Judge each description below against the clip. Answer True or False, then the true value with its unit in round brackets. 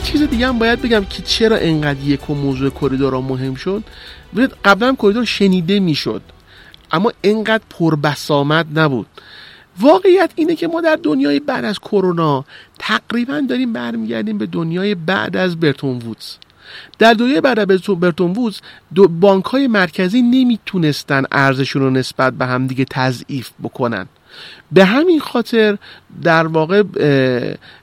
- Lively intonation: True (8.8 semitones)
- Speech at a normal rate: True (140 wpm)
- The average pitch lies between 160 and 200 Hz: True (190 Hz)